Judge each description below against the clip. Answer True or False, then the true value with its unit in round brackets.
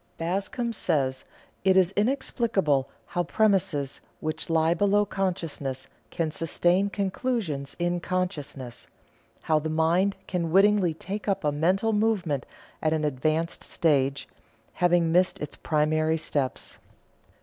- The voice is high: False (170 Hz)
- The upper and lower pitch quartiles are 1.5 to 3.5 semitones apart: False (4.2 semitones)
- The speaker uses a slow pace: True (120 wpm)